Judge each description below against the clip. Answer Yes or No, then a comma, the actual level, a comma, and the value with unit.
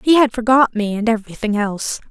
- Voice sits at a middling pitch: No, high, 225 Hz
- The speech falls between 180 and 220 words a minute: Yes, average, 200 wpm